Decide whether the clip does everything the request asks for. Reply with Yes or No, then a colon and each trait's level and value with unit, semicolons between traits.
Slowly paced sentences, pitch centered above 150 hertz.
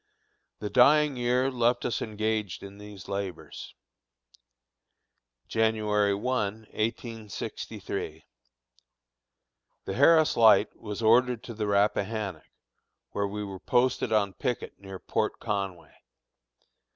No: slow, 105 wpm; low, 110 Hz